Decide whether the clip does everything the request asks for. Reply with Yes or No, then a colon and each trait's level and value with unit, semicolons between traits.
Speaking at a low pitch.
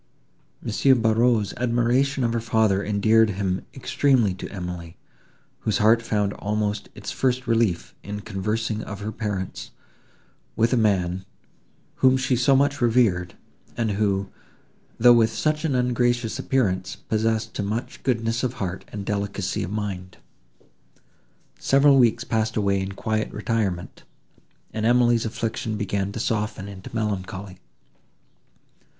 Yes: low, 110 Hz